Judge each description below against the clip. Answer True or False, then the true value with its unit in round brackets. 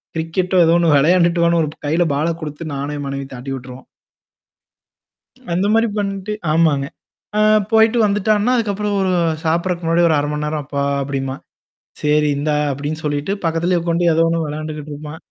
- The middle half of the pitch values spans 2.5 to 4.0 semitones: True (3.4 semitones)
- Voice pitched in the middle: True (160 Hz)